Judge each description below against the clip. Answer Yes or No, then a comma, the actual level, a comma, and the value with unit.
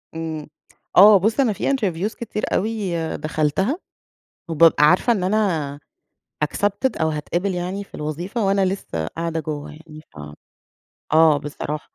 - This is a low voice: No, medium, 175 Hz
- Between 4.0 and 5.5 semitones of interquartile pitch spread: Yes, average, 4.8 semitones